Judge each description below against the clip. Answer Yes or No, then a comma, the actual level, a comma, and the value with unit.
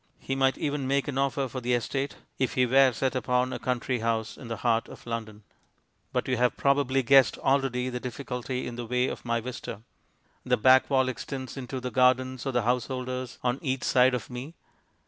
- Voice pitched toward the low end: Yes, low, 125 Hz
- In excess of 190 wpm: Yes, fast, 205 wpm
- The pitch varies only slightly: Yes, narrow, 1.5 semitones